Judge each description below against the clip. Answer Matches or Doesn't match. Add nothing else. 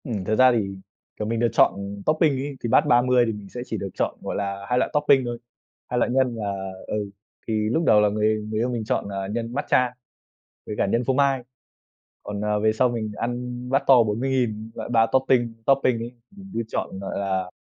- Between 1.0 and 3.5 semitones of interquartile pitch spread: Matches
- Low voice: Matches